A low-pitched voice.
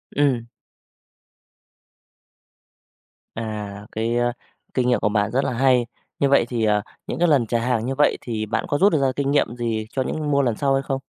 Yes: low, 125 Hz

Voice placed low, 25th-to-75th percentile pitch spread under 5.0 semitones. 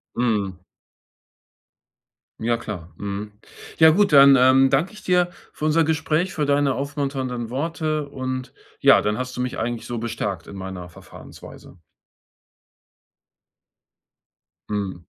No: low, 130 Hz; wide, 6.1 semitones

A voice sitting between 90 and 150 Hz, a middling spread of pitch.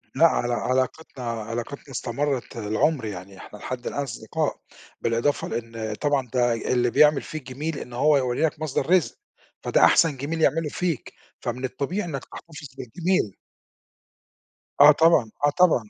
Yes: low, 135 Hz; average, 4.5 semitones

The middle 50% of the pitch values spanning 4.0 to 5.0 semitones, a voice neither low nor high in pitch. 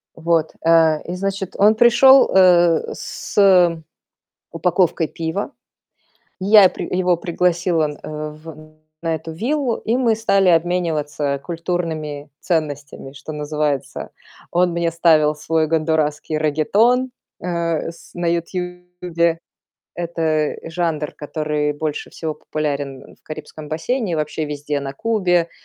No: average, 2.7 semitones; medium, 165 Hz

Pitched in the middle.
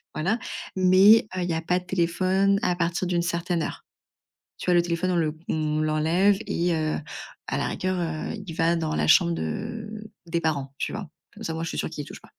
Yes: medium, 170 Hz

